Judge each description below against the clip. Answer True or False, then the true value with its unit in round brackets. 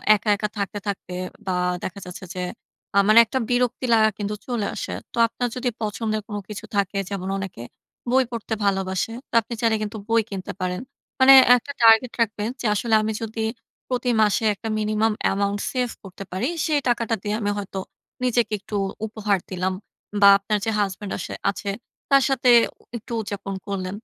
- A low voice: False (210 Hz)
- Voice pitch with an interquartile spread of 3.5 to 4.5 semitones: False (2.7 semitones)